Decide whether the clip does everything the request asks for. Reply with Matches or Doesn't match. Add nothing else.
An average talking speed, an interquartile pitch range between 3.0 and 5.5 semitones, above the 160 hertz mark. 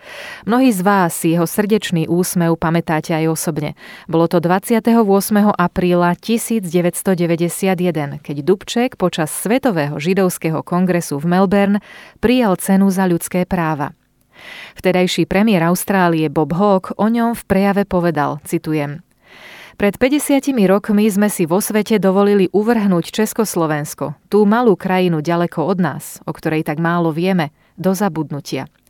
Matches